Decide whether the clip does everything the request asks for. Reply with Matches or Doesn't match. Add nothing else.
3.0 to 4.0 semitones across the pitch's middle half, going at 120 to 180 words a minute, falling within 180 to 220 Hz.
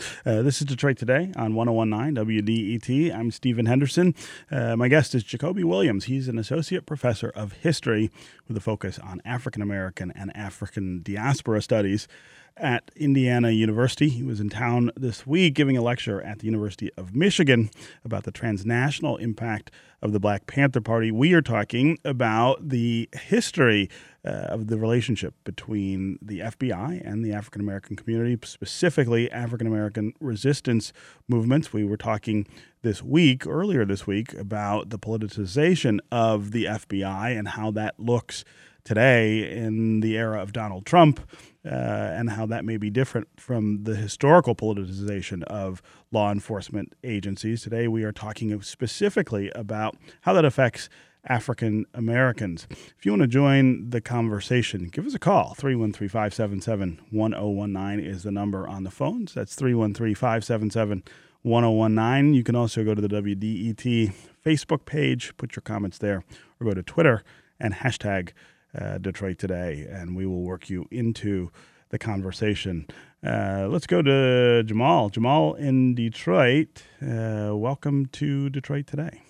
Doesn't match